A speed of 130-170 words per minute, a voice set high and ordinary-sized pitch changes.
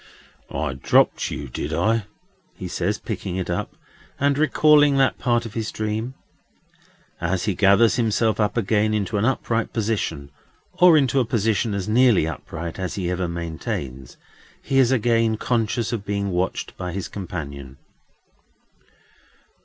No: average, 145 wpm; low, 105 Hz; average, 4.6 semitones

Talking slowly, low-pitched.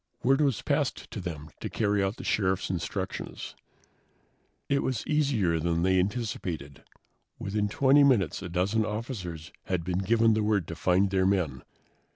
No: average, 160 wpm; very low, 95 Hz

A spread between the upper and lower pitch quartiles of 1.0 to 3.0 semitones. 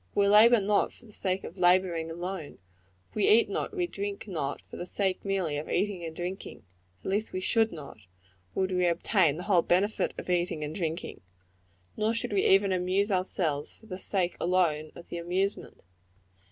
Yes: average, 2.7 semitones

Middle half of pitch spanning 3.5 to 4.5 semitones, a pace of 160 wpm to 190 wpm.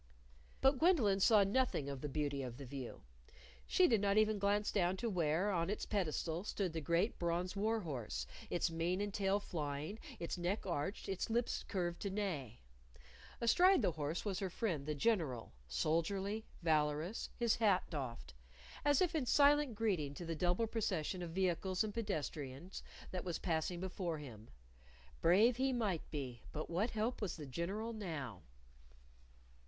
No: wide, 5.4 semitones; average, 165 wpm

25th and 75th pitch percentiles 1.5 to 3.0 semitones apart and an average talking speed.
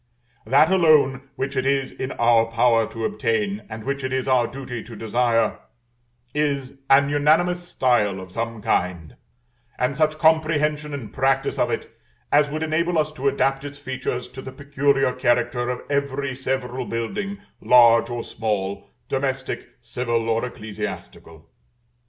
No: average, 3.6 semitones; average, 150 wpm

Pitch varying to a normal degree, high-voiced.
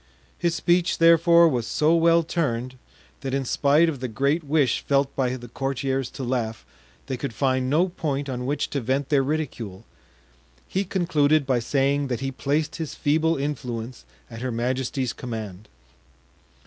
No: average, 3.7 semitones; low, 135 Hz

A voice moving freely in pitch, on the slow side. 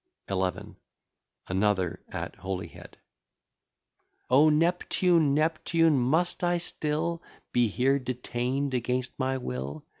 Yes: wide, 5.7 semitones; slow, 95 wpm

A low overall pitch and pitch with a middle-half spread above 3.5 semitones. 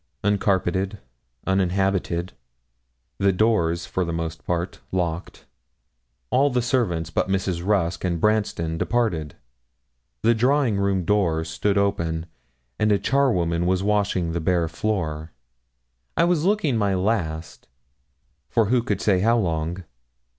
Yes: very low, 95 Hz; average, 4.2 semitones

